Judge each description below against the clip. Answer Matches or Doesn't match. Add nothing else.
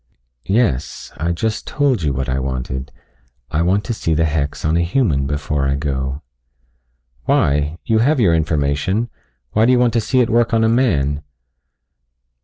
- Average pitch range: Doesn't match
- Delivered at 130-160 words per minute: Doesn't match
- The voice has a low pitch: Matches